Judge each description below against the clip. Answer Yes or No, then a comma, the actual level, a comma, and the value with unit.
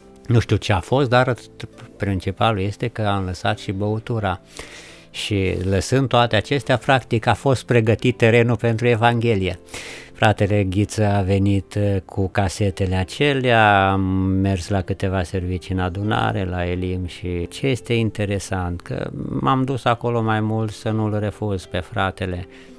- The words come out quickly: No, average, 145 wpm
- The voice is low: Yes, low, 105 Hz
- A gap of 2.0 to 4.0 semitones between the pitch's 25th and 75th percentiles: Yes, average, 3.5 semitones